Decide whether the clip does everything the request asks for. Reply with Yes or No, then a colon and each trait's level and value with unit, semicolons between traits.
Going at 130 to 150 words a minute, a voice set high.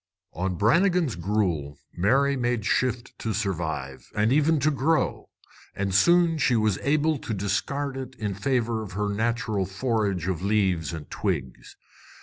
No: average, 145 wpm; low, 110 Hz